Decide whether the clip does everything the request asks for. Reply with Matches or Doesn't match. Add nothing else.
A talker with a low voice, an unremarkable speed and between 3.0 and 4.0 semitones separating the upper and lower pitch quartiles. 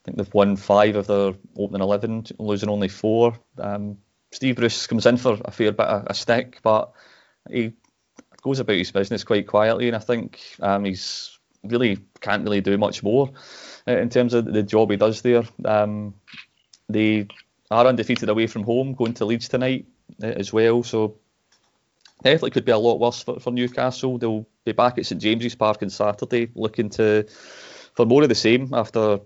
Doesn't match